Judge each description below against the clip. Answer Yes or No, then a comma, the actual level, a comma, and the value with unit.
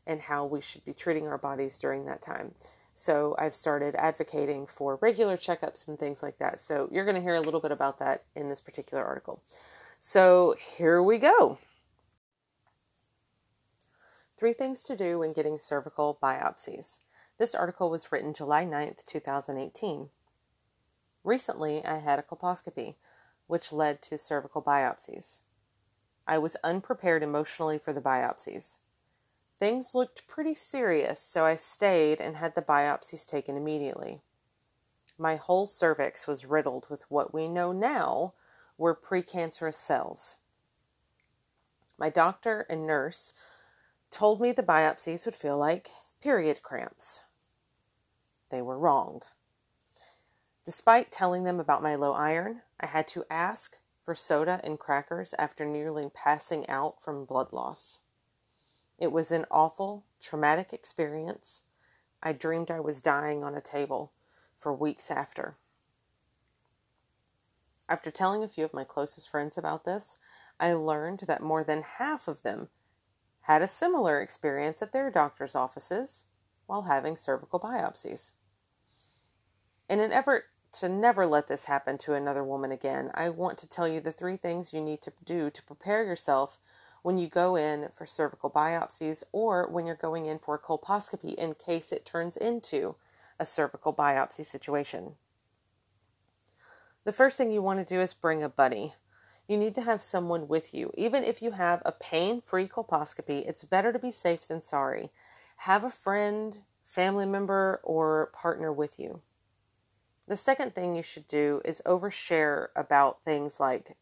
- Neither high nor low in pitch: Yes, medium, 155 Hz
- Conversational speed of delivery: Yes, average, 150 wpm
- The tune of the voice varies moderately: Yes, average, 3.9 semitones